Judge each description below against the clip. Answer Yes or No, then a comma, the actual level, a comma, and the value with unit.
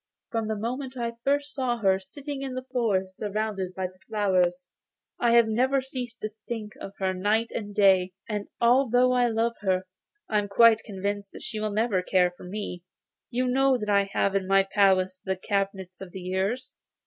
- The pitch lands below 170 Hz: No, high, 210 Hz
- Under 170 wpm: No, average, 195 wpm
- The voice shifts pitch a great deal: No, average, 3.8 semitones